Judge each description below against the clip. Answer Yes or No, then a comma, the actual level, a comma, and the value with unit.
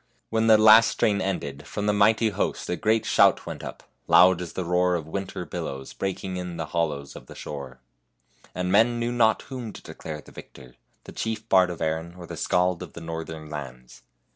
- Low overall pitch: Yes, very low, 90 Hz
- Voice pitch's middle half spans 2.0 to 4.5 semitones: No, average, 5.0 semitones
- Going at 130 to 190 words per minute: No, fast, 205 wpm